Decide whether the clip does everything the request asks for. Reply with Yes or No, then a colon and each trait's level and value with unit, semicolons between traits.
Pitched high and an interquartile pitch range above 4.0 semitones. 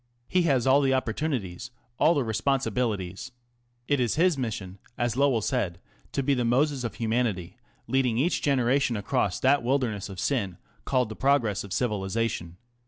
No: low, 120 Hz; average, 4.7 semitones